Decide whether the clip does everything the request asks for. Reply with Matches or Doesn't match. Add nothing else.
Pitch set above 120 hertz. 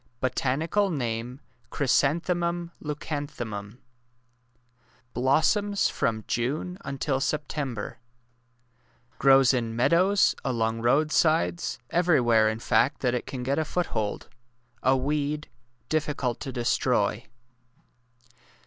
Matches